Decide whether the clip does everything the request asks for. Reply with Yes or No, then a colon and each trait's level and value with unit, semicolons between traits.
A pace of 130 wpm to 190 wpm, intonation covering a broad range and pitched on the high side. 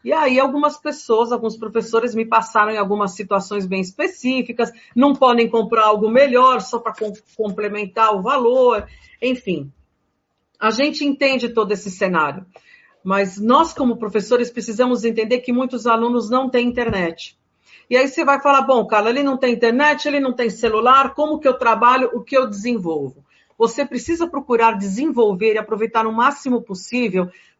No: average, 160 wpm; average, 3.2 semitones; high, 235 Hz